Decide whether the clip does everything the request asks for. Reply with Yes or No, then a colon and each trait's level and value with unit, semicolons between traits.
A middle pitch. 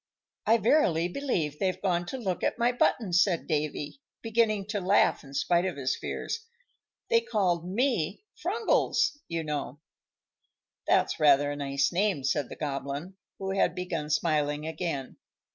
Yes: medium, 175 Hz